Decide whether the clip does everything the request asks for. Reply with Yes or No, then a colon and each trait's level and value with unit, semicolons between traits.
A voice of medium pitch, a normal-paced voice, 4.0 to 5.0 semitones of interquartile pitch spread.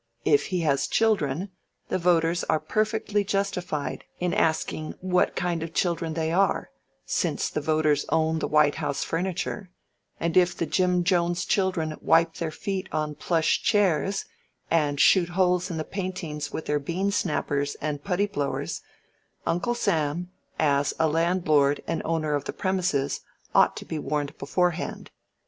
No: medium, 165 Hz; average, 155 wpm; average, 3.4 semitones